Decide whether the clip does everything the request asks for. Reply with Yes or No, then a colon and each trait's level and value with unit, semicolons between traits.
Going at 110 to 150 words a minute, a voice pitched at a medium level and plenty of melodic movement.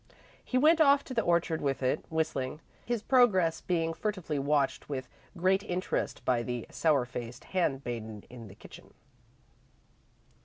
Yes: average, 145 wpm; medium, 160 Hz; wide, 6.7 semitones